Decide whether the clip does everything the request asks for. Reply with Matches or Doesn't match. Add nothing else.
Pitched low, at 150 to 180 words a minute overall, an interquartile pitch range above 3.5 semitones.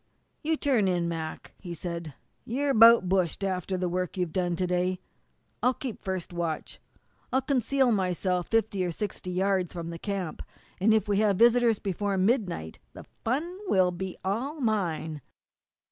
Doesn't match